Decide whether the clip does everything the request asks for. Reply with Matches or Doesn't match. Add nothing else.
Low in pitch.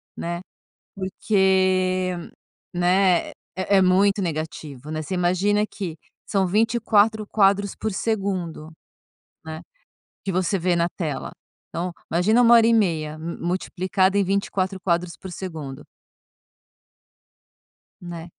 Doesn't match